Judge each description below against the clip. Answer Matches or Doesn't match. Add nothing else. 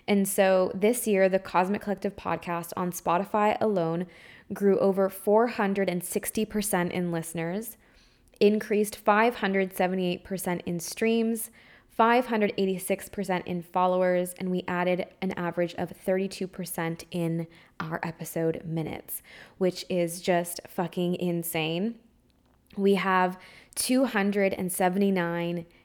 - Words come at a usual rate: Doesn't match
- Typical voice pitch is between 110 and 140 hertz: Doesn't match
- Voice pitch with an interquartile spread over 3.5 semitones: Doesn't match